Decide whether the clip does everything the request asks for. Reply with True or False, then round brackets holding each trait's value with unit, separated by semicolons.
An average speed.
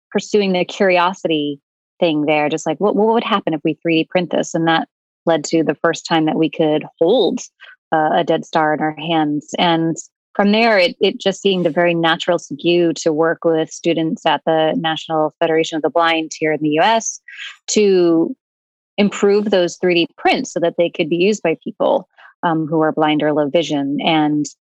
True (195 wpm)